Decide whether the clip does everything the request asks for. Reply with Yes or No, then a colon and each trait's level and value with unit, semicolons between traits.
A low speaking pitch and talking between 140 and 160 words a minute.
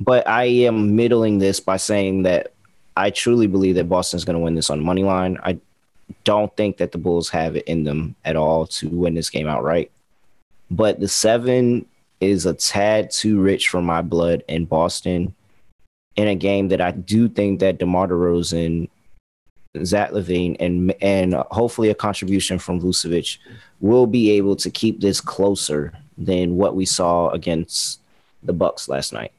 No: very low, 95 Hz; average, 175 wpm